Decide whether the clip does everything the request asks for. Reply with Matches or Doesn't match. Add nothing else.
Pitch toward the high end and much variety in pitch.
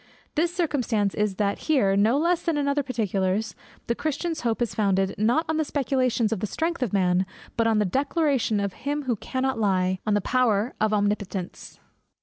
Matches